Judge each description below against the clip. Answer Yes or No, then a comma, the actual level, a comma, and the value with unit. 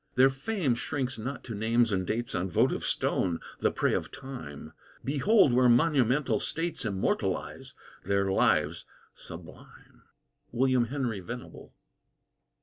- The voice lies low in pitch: Yes, low, 120 Hz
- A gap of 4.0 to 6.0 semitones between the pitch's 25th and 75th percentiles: Yes, average, 4.5 semitones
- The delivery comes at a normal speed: No, slow, 125 wpm